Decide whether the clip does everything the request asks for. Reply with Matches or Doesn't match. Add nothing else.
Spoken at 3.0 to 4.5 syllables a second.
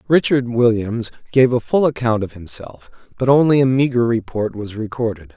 Doesn't match